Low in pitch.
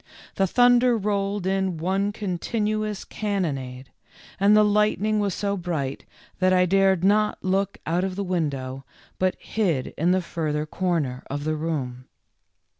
No: medium, 185 Hz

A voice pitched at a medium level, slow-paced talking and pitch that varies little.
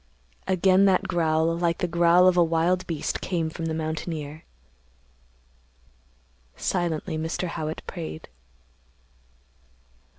Yes: medium, 165 Hz; slow, 105 wpm; narrow, 2.1 semitones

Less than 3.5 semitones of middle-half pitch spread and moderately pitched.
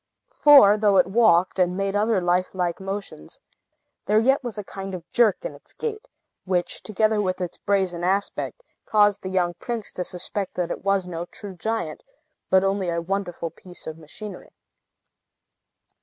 No: average, 2.8 semitones; high, 195 Hz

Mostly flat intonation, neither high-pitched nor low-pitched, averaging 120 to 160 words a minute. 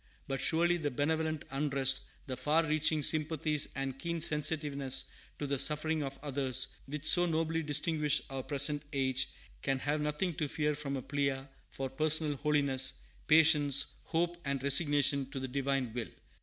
Yes: narrow, 2.3 semitones; medium, 145 Hz; average, 155 wpm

